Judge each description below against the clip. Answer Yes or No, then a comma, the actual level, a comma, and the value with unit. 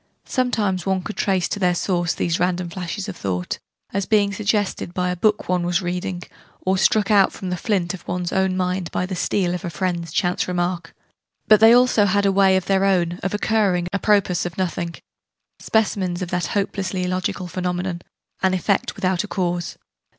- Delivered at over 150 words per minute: Yes, average, 195 wpm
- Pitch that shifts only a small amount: Yes, narrow, 2.0 semitones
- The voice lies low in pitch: No, medium, 185 Hz